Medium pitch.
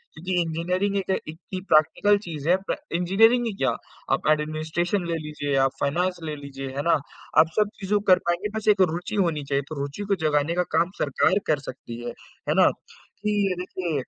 Yes: medium, 170 Hz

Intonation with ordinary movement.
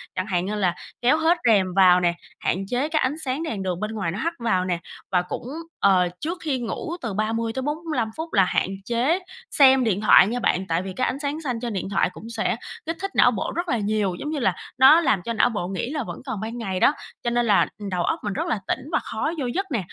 No: wide, 6.2 semitones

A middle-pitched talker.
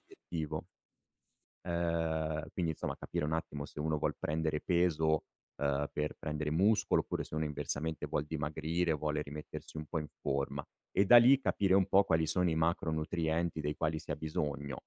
No: very low, 80 Hz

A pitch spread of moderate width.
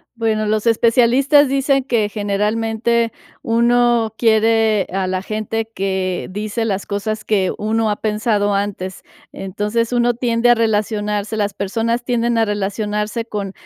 No: narrow, 2.1 semitones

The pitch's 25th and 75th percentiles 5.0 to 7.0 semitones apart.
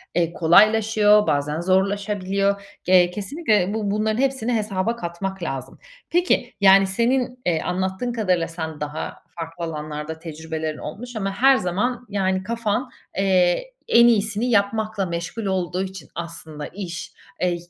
No: average, 4.2 semitones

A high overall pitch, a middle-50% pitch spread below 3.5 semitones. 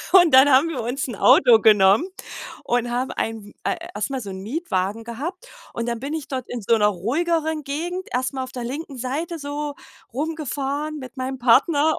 No: very high, 265 Hz; average, 4.4 semitones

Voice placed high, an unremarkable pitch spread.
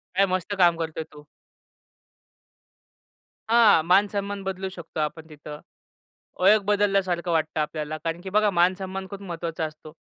No: medium, 180 Hz; average, 3.6 semitones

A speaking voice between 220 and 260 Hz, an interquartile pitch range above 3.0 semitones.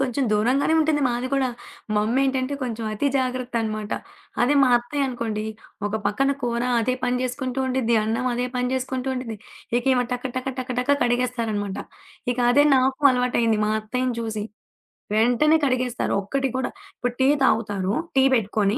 No: very high, 250 Hz; narrow, 2.4 semitones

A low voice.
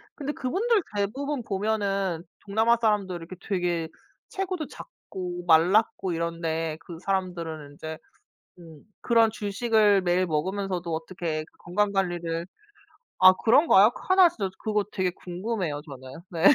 No: medium, 185 Hz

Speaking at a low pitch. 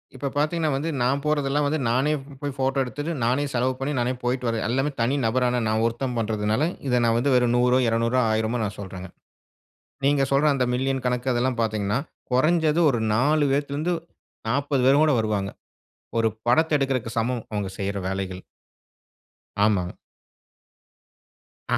Yes: low, 125 Hz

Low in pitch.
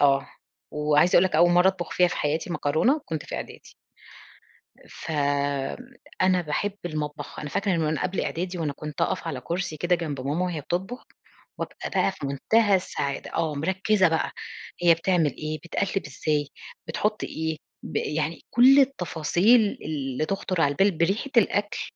No: medium, 170 Hz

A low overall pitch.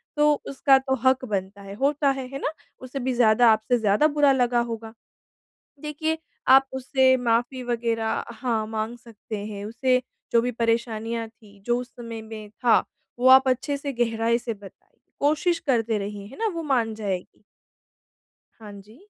No: high, 235 Hz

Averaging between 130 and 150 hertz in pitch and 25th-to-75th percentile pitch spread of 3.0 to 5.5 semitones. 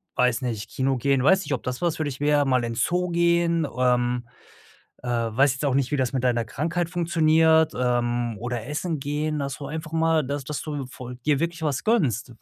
Yes: medium, 140 Hz; average, 4.4 semitones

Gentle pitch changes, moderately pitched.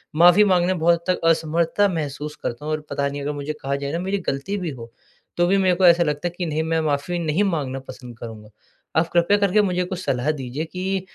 No: average, 4.1 semitones; medium, 165 Hz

